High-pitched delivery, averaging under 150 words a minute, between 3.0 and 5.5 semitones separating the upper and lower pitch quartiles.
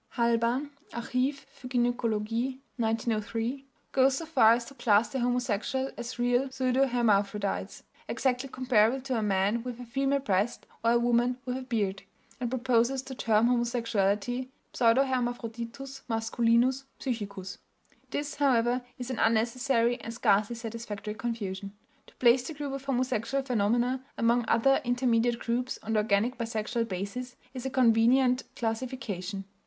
No: high, 240 Hz; average, 140 wpm; narrow, 2.4 semitones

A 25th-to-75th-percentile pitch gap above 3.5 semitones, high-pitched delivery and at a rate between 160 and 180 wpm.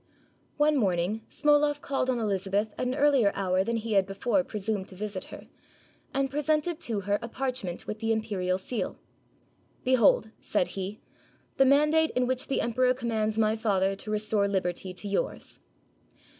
Yes: average, 4.6 semitones; high, 220 Hz; average, 170 wpm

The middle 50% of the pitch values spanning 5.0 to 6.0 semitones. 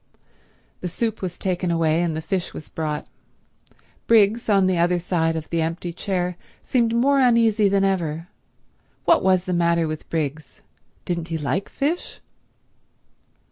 No: average, 3.5 semitones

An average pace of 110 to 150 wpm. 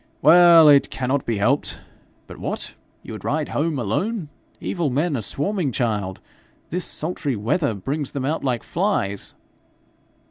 Yes: average, 145 wpm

